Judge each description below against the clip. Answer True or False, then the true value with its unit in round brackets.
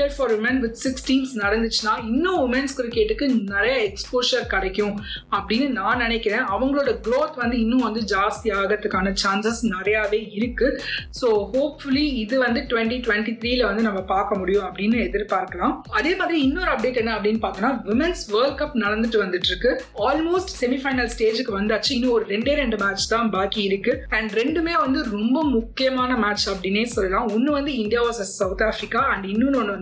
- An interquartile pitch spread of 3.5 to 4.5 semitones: True (4.0 semitones)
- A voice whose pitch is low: False (230 Hz)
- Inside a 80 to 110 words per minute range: False (125 wpm)